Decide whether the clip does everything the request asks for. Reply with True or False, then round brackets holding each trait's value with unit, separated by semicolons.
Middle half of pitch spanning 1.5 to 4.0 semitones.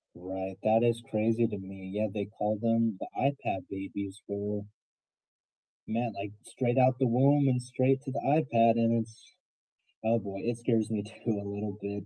True (2.9 semitones)